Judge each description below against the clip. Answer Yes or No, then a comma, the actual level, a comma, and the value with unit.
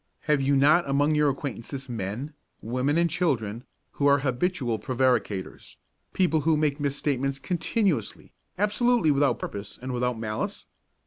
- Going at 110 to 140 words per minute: Yes, slow, 135 wpm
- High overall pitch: No, medium, 140 Hz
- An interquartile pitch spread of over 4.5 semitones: No, average, 3.8 semitones